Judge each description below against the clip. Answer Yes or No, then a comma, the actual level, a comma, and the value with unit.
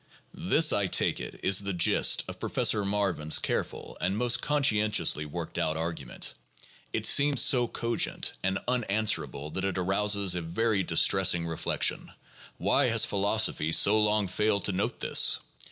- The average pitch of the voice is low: Yes, low, 100 Hz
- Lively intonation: No, average, 3.9 semitones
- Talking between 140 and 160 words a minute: Yes, average, 155 wpm